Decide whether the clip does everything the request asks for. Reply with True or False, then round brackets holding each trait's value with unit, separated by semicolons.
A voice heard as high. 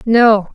True (220 Hz)